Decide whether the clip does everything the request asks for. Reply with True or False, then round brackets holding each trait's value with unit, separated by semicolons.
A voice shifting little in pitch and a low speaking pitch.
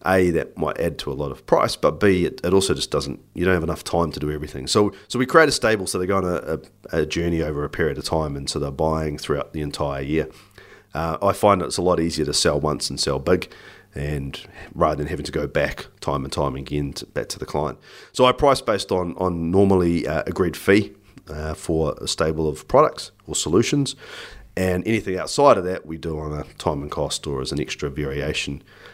False (3.8 semitones; 80 Hz)